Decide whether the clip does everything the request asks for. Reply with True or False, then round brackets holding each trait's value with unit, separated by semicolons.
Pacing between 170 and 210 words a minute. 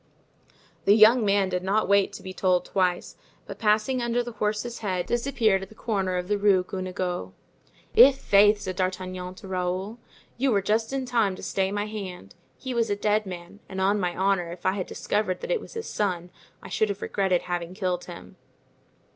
True (195 wpm)